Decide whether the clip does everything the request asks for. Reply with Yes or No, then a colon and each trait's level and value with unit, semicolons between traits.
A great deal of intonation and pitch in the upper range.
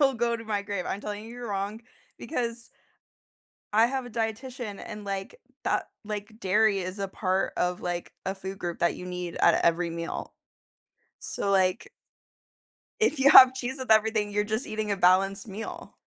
No: average, 3.3 semitones; high, 210 Hz